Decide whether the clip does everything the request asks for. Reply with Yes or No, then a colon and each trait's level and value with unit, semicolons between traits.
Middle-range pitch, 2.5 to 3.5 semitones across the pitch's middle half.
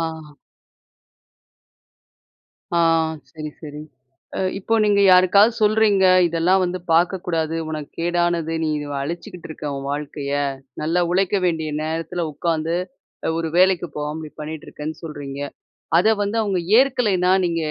Yes: medium, 170 Hz; average, 3.0 semitones